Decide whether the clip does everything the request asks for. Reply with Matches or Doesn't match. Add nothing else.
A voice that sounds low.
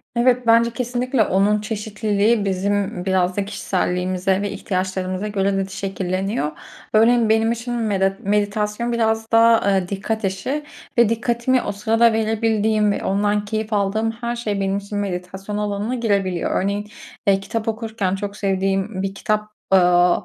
Doesn't match